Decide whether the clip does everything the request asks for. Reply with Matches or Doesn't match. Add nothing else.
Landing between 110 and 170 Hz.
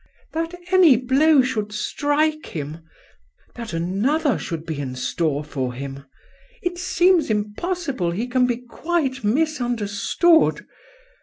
Doesn't match